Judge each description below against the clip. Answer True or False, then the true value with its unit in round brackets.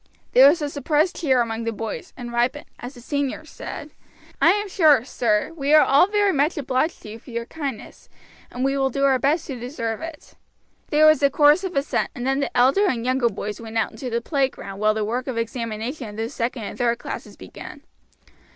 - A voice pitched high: True (260 Hz)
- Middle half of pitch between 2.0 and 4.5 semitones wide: True (4.1 semitones)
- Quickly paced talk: True (220 wpm)